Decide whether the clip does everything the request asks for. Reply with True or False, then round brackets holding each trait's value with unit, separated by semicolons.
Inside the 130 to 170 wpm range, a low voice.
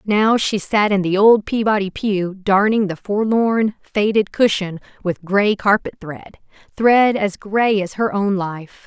False (160 wpm; 205 Hz)